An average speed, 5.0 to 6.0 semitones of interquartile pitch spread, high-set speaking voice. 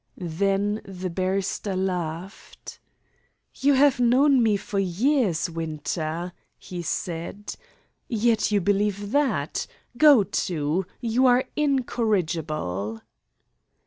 No: slow, 95 wpm; wide, 5.5 semitones; high, 195 Hz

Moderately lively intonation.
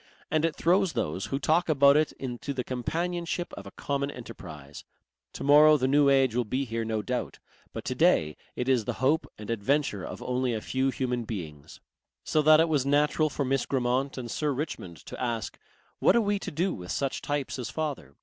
Yes: average, 4.4 semitones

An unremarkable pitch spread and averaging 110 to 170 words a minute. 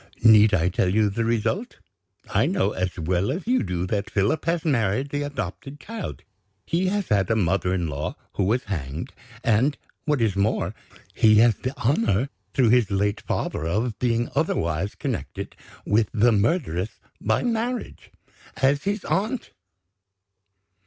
No: wide, 6.7 semitones; average, 155 wpm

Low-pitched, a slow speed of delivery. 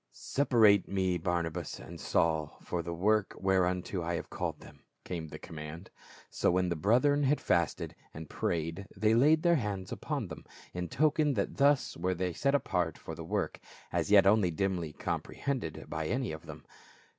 No: very low, 90 Hz; average, 180 wpm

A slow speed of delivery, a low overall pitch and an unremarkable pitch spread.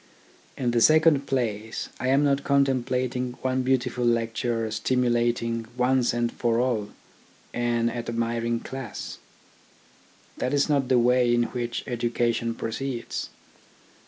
No: slow, 120 wpm; low, 120 Hz; narrow, 1.7 semitones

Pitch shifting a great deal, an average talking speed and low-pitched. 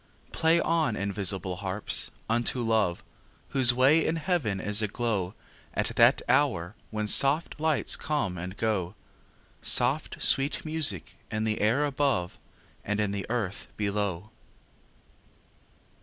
No: wide, 5.8 semitones; slow, 125 wpm; low, 110 Hz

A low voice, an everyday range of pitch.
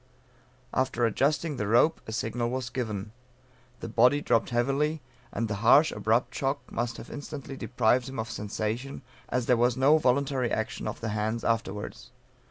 Yes: low, 120 Hz; average, 3.3 semitones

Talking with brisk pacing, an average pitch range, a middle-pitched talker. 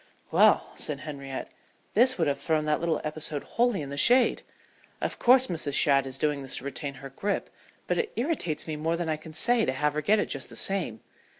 No: fast, 220 wpm; wide, 5.8 semitones; medium, 155 Hz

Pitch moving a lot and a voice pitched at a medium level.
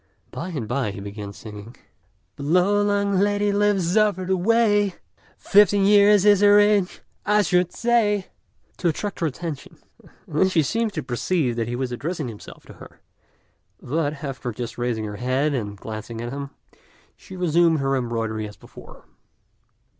Yes: wide, 8.9 semitones; medium, 165 Hz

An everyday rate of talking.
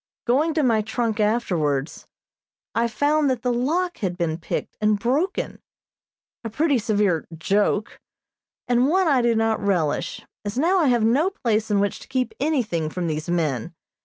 Yes: average, 165 wpm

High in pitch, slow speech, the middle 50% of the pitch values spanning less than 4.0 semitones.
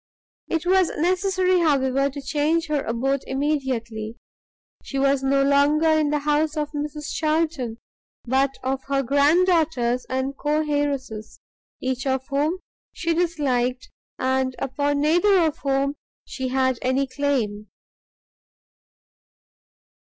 Yes: very high, 280 Hz; slow, 125 wpm; average, 2.7 semitones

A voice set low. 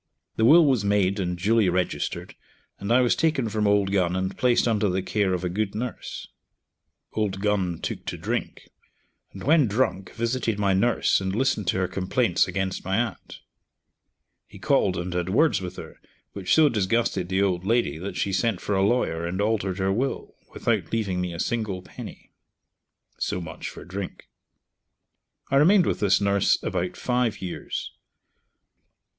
Yes: low, 100 Hz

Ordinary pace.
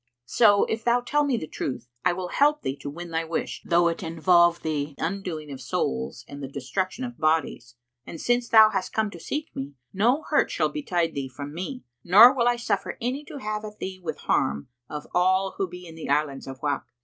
No: fast, 220 wpm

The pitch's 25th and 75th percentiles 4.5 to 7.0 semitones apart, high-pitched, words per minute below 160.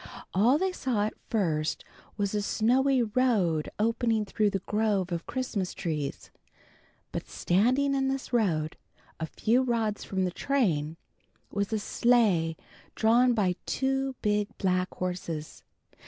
Yes: average, 5.2 semitones; high, 210 Hz; slow, 135 wpm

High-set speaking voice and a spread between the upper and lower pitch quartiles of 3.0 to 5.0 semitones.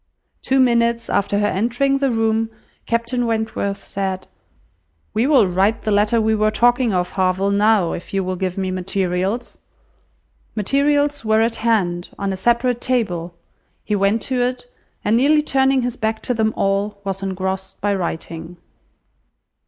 Yes: high, 215 Hz; average, 3.8 semitones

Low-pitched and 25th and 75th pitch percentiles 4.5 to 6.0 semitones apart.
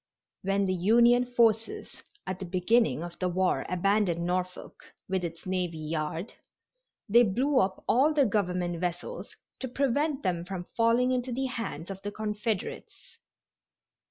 No: high, 195 Hz; average, 5.0 semitones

